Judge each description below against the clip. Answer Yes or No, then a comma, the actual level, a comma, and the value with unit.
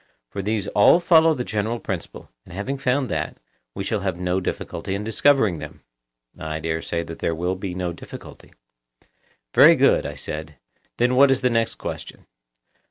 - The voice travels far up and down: Yes, wide, 6.0 semitones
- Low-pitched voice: Yes, low, 100 Hz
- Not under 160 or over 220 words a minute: Yes, average, 175 wpm